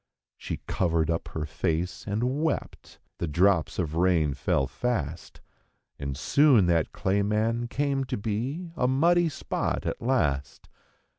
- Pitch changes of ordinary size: No, wide, 8.2 semitones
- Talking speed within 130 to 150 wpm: Yes, average, 140 wpm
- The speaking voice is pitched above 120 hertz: No, low, 100 Hz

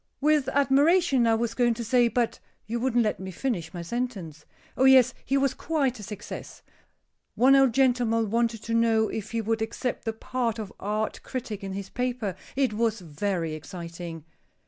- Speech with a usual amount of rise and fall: Yes, average, 3.7 semitones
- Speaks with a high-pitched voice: Yes, high, 230 Hz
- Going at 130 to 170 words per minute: No, average, 180 wpm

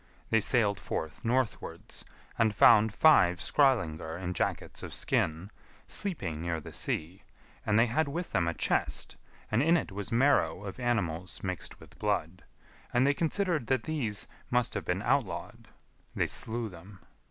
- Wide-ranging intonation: Yes, wide, 6.5 semitones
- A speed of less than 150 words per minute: No, average, 155 wpm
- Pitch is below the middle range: Yes, low, 105 Hz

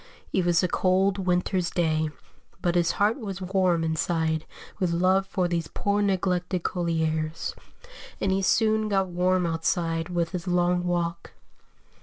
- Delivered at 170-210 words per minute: No, average, 145 wpm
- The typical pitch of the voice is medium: Yes, medium, 180 Hz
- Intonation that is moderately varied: No, narrow, 2.1 semitones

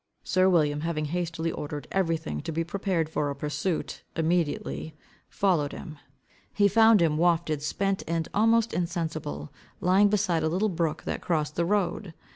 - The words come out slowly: No, average, 155 wpm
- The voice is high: No, medium, 165 Hz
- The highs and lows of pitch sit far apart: No, average, 3.4 semitones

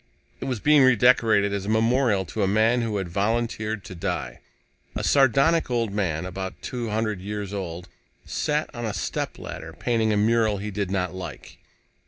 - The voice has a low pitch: Yes, low, 105 Hz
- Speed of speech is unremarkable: Yes, average, 175 wpm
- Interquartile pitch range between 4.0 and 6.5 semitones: No, average, 3.5 semitones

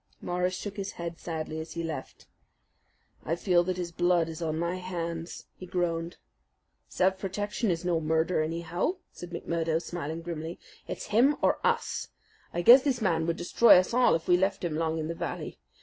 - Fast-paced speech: No, average, 185 wpm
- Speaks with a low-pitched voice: No, medium, 175 Hz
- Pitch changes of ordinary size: No, narrow, 2.1 semitones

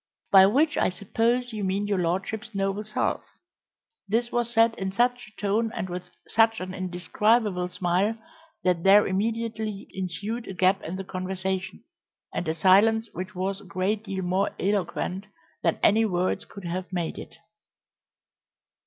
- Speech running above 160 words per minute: No, average, 155 wpm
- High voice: Yes, high, 195 Hz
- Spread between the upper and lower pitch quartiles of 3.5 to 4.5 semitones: No, average, 3.1 semitones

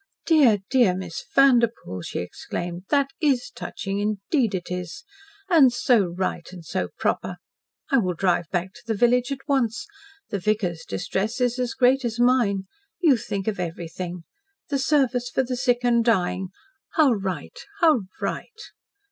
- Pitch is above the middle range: Yes, high, 225 Hz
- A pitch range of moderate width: No, wide, 5.7 semitones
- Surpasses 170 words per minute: No, average, 155 wpm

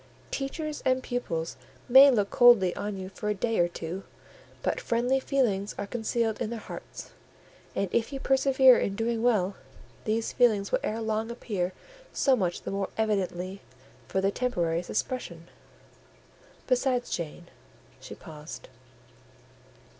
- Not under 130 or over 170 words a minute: Yes, average, 140 wpm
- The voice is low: No, high, 220 Hz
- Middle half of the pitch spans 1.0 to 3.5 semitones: No, average, 4.5 semitones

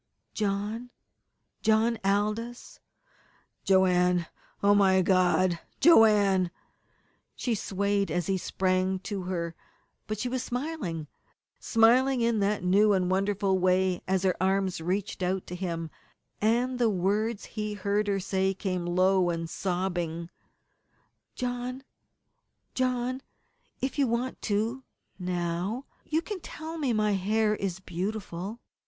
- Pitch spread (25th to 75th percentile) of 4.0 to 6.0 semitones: No, average, 3.5 semitones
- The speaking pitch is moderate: No, high, 200 Hz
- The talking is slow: Yes, slow, 125 wpm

